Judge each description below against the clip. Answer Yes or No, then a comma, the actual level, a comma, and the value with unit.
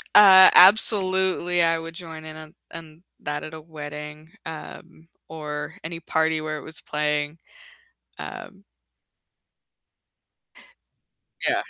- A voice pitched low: No, medium, 160 Hz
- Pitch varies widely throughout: No, narrow, 2.4 semitones